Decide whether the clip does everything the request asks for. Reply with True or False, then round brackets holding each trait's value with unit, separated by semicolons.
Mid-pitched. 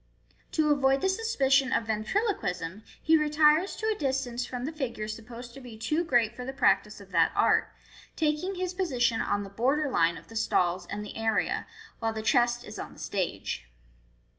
False (245 Hz)